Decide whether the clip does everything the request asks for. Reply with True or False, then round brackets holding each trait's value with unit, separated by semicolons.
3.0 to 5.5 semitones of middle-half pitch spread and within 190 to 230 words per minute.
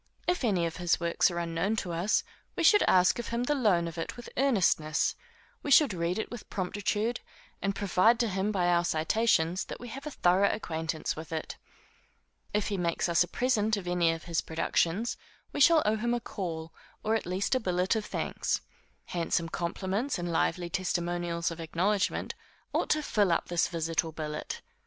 True (4.5 semitones; 195 wpm)